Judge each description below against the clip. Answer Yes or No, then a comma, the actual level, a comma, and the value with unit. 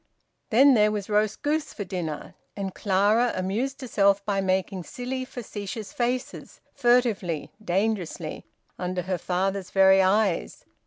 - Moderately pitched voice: No, high, 200 Hz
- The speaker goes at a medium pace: No, slow, 125 wpm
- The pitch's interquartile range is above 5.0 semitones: No, average, 4.0 semitones